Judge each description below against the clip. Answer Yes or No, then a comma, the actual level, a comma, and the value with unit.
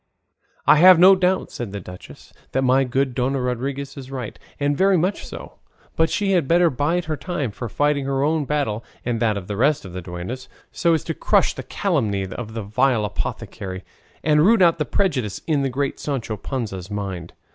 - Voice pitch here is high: No, low, 135 Hz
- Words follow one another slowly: No, average, 200 wpm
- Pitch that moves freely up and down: Yes, wide, 6.3 semitones